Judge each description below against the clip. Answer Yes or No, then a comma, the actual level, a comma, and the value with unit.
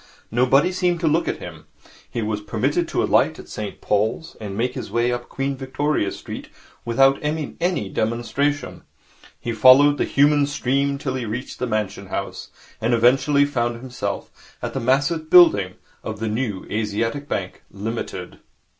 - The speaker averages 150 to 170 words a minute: Yes, average, 160 wpm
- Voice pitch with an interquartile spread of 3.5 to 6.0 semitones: Yes, average, 4.7 semitones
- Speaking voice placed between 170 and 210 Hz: No, low, 125 Hz